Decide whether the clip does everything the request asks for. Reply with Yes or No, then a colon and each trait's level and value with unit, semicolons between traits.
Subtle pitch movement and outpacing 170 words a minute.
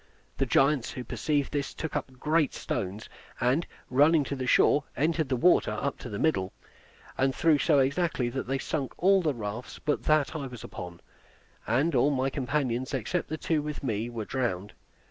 No: average, 3.8 semitones; average, 185 wpm